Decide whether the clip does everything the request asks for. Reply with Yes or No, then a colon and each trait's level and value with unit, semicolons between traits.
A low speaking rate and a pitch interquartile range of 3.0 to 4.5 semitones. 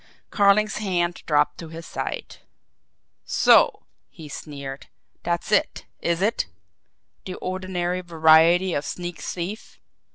No: slow, 110 wpm; narrow, 2.6 semitones